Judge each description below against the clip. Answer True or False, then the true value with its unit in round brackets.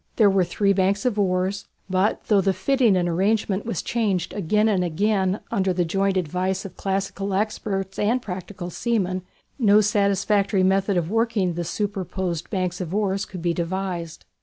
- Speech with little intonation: True (2.1 semitones)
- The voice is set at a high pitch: True (195 Hz)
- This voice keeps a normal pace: True (165 wpm)